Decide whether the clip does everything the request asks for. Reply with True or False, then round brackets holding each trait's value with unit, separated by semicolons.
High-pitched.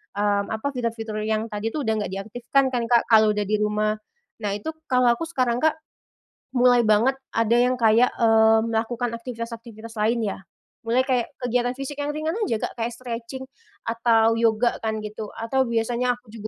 True (230 Hz)